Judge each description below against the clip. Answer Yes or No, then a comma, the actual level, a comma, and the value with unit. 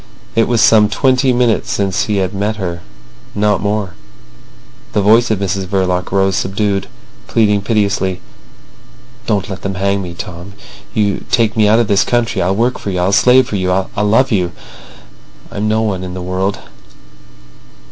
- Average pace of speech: Yes, average, 165 wpm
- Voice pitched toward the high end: No, low, 100 Hz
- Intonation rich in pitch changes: No, narrow, 2.5 semitones